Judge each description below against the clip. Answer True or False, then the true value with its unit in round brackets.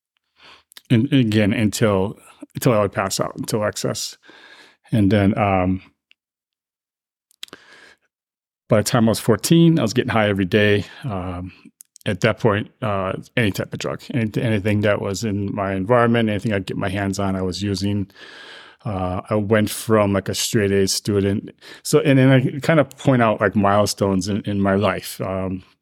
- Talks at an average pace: True (170 wpm)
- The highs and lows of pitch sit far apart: False (2.9 semitones)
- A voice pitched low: True (105 Hz)